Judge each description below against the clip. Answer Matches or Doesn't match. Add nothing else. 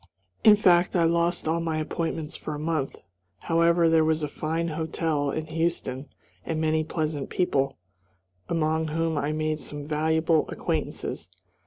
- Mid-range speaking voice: Matches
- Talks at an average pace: Matches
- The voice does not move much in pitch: Matches